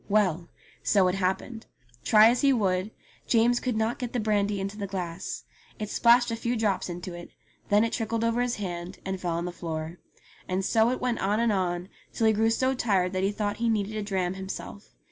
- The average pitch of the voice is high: Yes, high, 205 Hz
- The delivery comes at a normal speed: No, fast, 220 wpm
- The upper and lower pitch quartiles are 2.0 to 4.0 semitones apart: Yes, average, 3.6 semitones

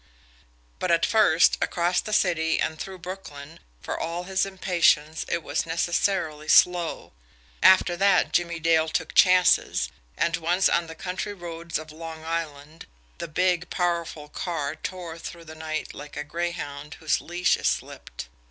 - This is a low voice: No, medium, 170 Hz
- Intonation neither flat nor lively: No, narrow, 2.1 semitones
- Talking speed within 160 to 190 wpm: No, average, 150 wpm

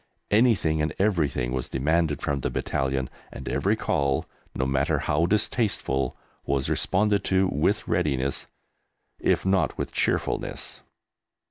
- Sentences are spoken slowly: Yes, slow, 125 wpm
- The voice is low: Yes, very low, 75 Hz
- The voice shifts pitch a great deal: Yes, wide, 6.0 semitones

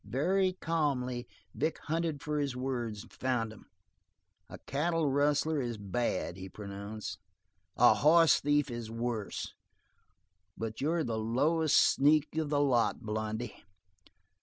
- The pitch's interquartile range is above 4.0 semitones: Yes, average, 5.2 semitones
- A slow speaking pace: Yes, slow, 125 wpm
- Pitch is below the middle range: Yes, low, 130 Hz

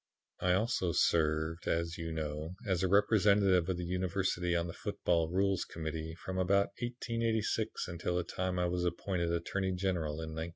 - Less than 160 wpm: No, average, 170 wpm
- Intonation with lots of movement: No, narrow, 2.6 semitones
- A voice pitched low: Yes, very low, 90 Hz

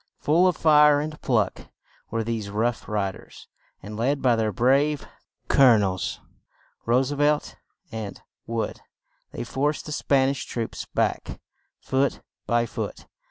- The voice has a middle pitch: No, low, 125 Hz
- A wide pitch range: No, average, 4.6 semitones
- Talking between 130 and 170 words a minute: Yes, average, 140 wpm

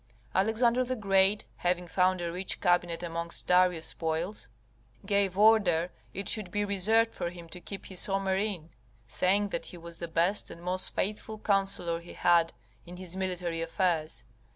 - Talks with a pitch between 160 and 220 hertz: Yes, medium, 185 Hz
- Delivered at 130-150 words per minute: No, average, 165 wpm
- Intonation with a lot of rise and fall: No, average, 2.7 semitones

